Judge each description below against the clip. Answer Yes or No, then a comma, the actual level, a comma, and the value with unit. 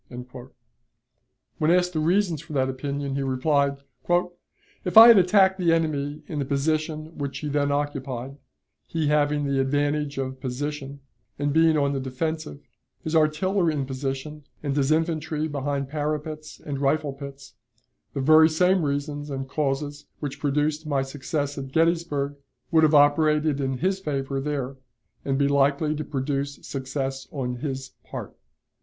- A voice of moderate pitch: Yes, medium, 145 Hz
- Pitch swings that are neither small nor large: No, narrow, 2.1 semitones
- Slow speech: No, average, 150 wpm